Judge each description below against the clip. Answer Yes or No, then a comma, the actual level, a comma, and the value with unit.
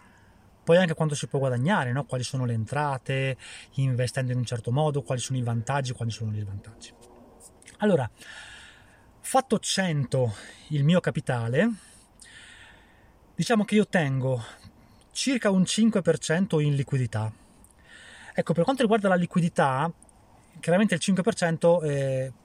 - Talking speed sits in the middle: Yes, average, 130 wpm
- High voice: No, medium, 140 Hz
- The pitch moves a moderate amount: No, wide, 6.4 semitones